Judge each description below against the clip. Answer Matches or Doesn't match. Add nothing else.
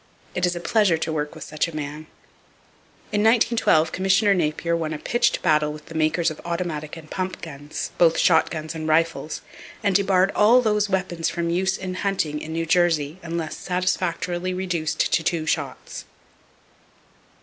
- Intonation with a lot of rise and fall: Doesn't match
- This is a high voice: Doesn't match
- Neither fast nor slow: Matches